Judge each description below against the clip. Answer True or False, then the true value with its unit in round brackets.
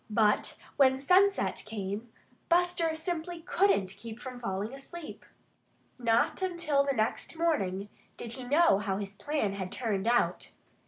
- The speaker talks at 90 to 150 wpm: True (140 wpm)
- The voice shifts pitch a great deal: True (8.0 semitones)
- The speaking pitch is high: True (250 Hz)